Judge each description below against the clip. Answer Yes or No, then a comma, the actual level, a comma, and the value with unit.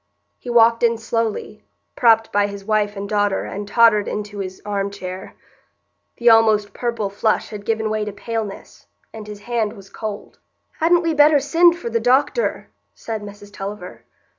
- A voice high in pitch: Yes, high, 215 Hz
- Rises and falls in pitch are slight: Yes, narrow, 2.2 semitones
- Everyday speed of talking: Yes, average, 165 wpm